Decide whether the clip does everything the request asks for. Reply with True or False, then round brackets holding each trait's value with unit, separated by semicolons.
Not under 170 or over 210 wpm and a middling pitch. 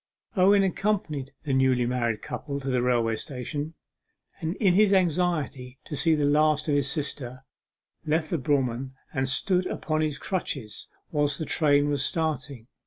False (160 wpm; 145 Hz)